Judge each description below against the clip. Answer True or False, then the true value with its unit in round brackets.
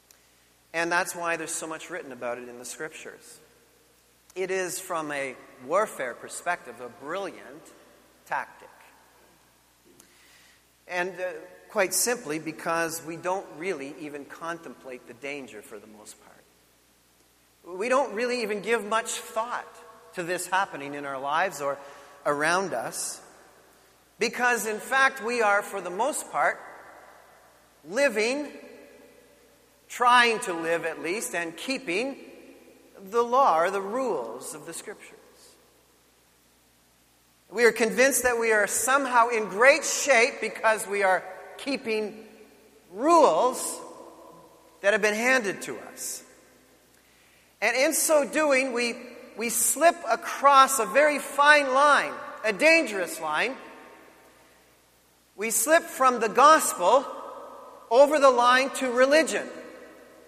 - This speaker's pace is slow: True (125 wpm)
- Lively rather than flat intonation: True (8.1 semitones)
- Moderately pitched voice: False (215 Hz)